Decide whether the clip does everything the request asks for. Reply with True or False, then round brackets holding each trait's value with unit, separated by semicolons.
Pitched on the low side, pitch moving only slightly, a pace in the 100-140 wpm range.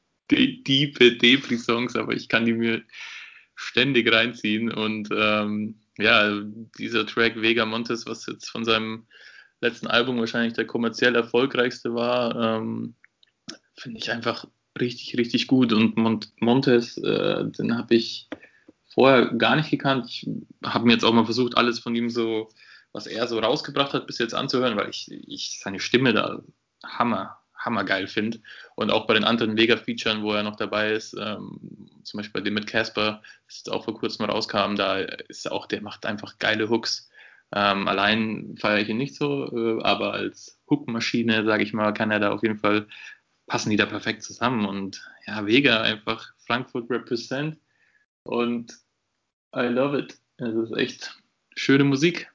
False (115 Hz; 1.8 semitones; 165 wpm)